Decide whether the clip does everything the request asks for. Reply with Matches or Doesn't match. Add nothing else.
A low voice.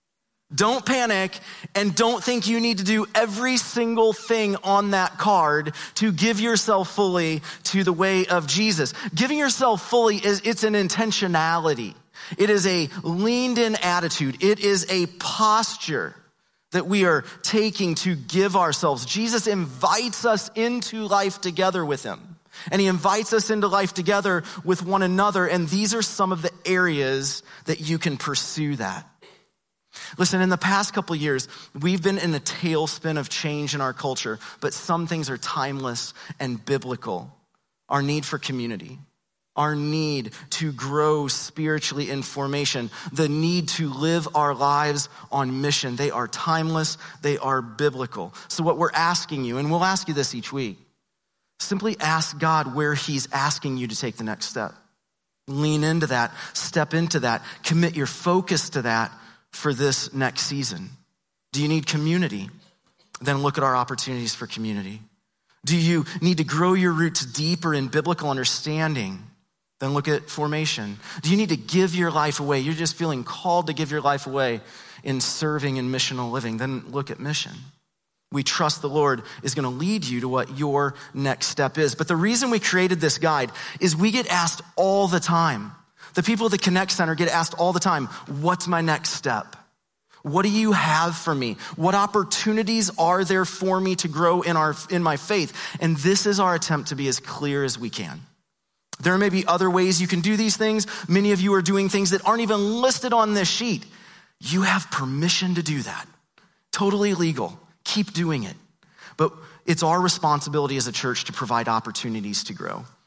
Doesn't match